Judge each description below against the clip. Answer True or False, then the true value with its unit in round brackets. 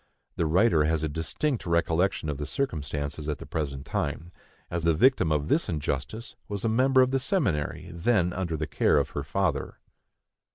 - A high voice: False (85 Hz)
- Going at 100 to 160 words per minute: False (180 wpm)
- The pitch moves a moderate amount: False (6.8 semitones)